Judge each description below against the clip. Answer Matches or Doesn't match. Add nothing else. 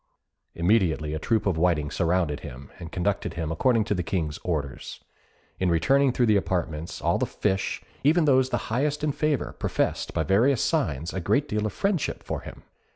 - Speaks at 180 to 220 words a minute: Matches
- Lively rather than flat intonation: Matches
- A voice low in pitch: Matches